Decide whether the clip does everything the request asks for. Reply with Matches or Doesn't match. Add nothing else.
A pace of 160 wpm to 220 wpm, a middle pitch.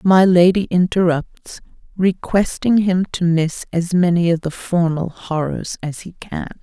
Doesn't match